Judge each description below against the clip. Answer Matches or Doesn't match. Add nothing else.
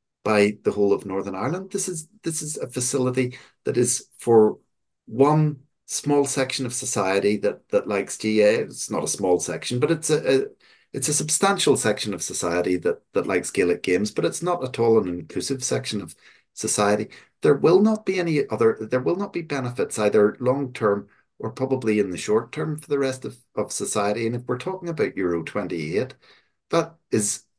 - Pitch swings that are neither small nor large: Doesn't match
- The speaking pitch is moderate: Doesn't match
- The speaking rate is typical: Matches